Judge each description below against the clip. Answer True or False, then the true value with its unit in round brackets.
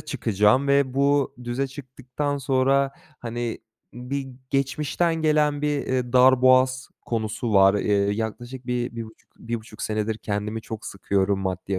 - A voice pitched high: False (125 Hz)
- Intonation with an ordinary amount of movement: True (3.9 semitones)